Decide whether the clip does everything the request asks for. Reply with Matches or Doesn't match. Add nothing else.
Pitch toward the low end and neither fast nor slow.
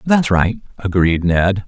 Matches